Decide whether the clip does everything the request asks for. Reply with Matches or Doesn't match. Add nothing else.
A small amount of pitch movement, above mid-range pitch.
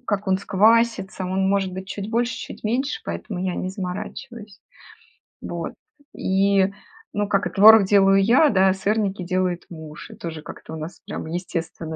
Matches